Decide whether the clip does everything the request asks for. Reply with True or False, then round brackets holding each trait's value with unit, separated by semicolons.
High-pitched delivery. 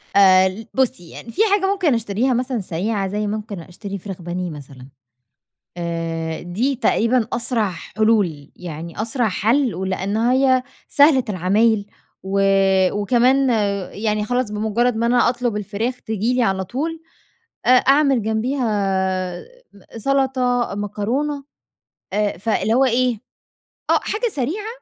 True (220 Hz)